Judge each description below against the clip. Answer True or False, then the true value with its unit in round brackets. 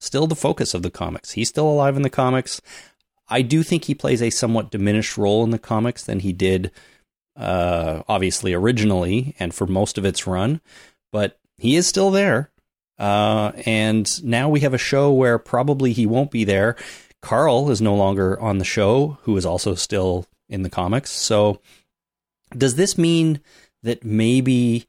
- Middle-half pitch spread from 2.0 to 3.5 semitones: False (5.6 semitones)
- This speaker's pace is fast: False (180 wpm)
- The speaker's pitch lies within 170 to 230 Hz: False (115 Hz)